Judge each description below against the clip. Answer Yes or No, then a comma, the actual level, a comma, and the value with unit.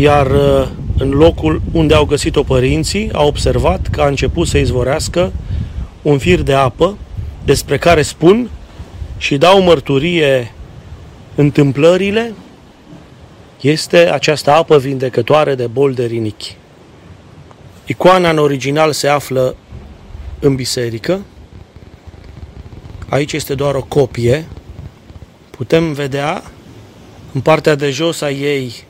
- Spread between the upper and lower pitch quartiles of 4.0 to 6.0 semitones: Yes, average, 4.4 semitones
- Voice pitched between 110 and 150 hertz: Yes, medium, 140 Hz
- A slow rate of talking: Yes, slow, 110 wpm